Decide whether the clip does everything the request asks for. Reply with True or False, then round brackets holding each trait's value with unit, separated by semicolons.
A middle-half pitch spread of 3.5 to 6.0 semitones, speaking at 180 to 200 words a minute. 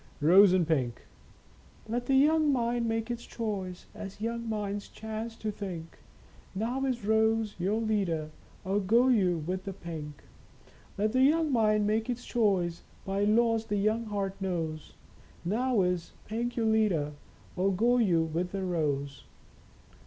False (4.1 semitones; 155 wpm)